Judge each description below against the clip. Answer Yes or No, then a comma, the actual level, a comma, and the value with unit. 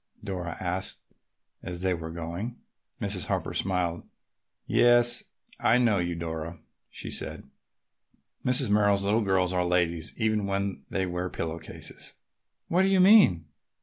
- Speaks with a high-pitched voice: No, very low, 95 Hz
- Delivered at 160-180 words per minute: No, average, 140 wpm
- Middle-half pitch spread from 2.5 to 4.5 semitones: Yes, average, 3.9 semitones